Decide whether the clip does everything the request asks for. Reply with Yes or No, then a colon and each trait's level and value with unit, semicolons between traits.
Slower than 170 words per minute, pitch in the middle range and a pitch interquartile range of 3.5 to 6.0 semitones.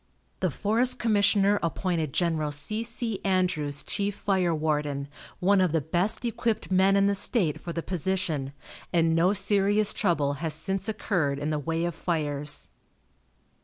Yes: average, 155 wpm; medium, 180 Hz; average, 4.6 semitones